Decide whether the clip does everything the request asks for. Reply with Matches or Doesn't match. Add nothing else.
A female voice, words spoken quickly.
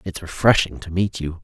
Doesn't match